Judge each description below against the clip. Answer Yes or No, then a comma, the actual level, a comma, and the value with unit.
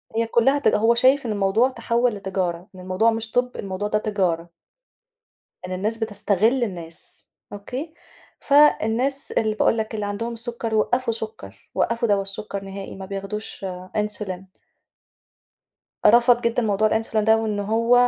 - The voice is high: Yes, high, 215 Hz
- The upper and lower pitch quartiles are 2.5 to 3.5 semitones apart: Yes, average, 2.9 semitones